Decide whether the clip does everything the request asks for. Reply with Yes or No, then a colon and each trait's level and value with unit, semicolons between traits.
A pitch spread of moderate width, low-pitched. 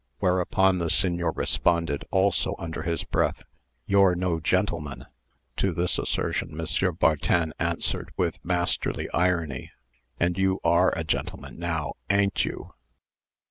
No: narrow, 2.1 semitones; very low, 85 Hz